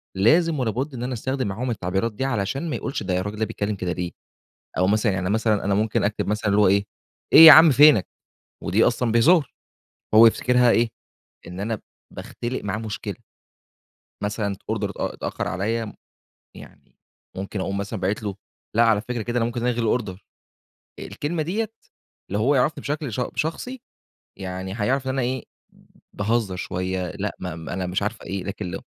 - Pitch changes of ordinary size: Yes, average, 4.2 semitones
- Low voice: Yes, low, 110 Hz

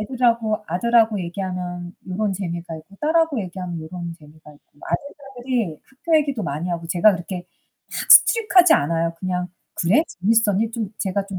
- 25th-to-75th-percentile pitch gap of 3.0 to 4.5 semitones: No, average, 5.2 semitones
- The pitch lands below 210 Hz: Yes, high, 190 Hz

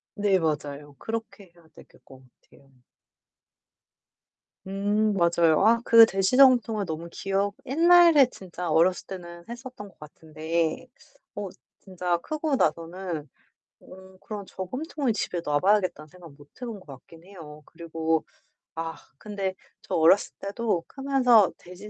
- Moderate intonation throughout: Yes, average, 4.9 semitones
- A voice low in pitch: No, high, 190 Hz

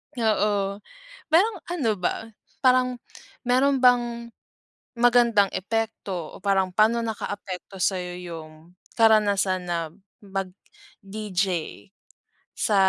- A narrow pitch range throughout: No, average, 4.0 semitones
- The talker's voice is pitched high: Yes, high, 210 Hz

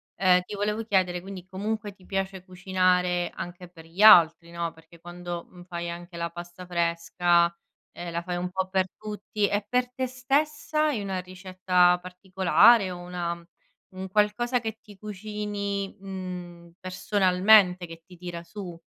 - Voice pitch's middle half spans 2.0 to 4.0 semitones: Yes, average, 2.7 semitones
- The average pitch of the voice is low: No, medium, 185 Hz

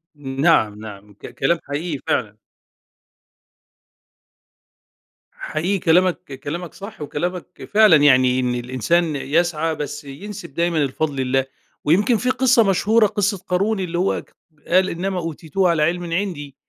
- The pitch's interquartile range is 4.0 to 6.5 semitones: Yes, average, 4.9 semitones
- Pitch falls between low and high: Yes, medium, 170 Hz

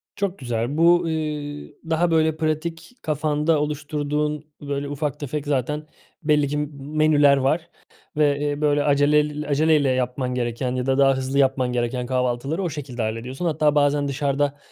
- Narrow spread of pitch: Yes, narrow, 2.1 semitones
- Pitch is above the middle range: No, medium, 145 Hz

